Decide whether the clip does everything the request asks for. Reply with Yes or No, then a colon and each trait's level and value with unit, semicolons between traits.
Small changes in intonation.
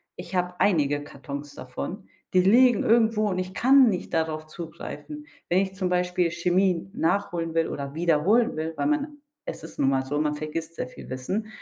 No: average, 4.5 semitones